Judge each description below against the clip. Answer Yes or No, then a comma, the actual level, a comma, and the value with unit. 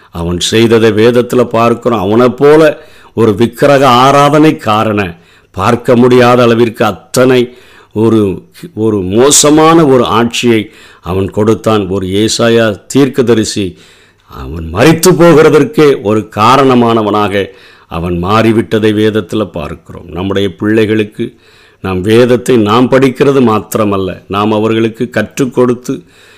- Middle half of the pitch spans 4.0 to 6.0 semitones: No, average, 3.3 semitones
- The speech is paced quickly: No, average, 100 wpm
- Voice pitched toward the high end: No, low, 115 Hz